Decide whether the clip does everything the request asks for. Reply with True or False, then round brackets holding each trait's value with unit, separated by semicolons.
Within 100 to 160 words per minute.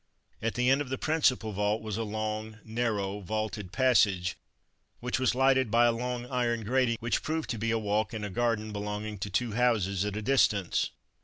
False (200 wpm)